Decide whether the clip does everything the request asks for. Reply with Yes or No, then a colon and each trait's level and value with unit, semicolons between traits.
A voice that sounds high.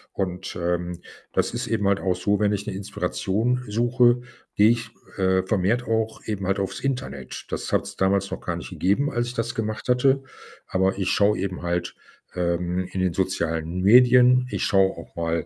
No: low, 100 Hz